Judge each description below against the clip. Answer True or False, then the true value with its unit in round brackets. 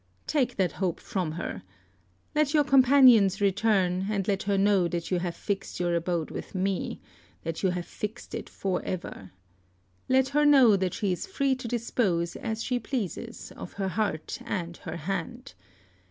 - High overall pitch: True (195 Hz)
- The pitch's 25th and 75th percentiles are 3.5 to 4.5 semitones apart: False (5.4 semitones)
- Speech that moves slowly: False (170 wpm)